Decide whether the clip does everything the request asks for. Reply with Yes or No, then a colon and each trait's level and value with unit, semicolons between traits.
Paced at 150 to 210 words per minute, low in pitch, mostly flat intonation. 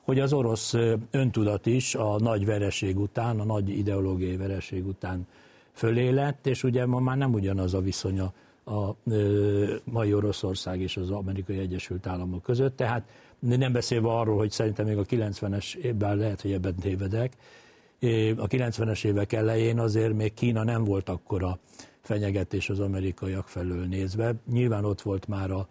No: fast, 155 wpm; low, 105 Hz; average, 3.2 semitones